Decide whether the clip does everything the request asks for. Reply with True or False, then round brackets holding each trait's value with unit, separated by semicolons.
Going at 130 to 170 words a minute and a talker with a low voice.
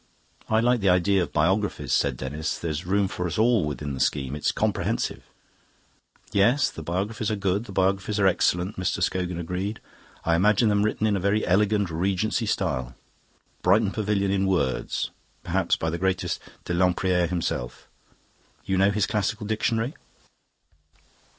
True (160 wpm; 95 Hz)